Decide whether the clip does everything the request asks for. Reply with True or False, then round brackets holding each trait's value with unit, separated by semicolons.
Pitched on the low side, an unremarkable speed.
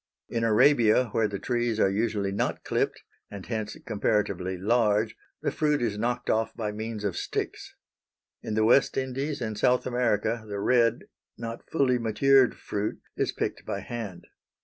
True (115 Hz; 160 wpm)